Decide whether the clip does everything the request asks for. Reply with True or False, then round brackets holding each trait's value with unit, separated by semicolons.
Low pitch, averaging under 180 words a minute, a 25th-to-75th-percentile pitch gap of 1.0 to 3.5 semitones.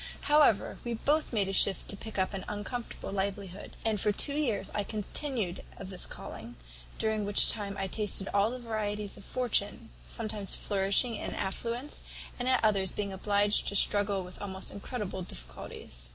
False (205 Hz; 170 wpm; 2.6 semitones)